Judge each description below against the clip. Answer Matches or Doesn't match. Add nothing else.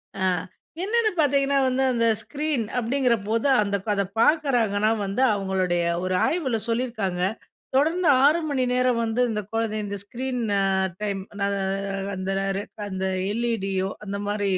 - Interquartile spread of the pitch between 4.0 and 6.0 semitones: Matches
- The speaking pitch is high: Matches